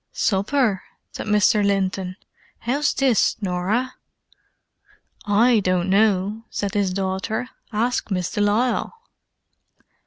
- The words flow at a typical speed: No, slow, 100 wpm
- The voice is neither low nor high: No, high, 205 Hz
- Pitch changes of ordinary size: Yes, average, 3.2 semitones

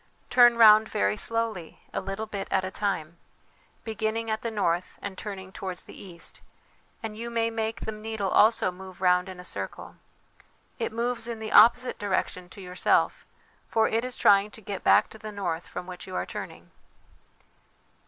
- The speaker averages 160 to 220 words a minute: Yes, average, 180 wpm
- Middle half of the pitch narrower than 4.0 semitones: Yes, average, 3.1 semitones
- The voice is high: Yes, high, 205 Hz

